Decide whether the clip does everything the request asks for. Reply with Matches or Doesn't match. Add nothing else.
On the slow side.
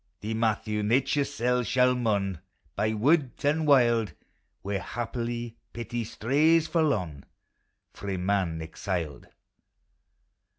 Matches